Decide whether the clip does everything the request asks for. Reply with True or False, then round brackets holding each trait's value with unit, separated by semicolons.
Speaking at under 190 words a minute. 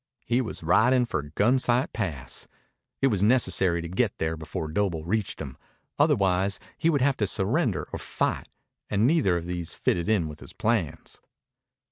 True (165 wpm)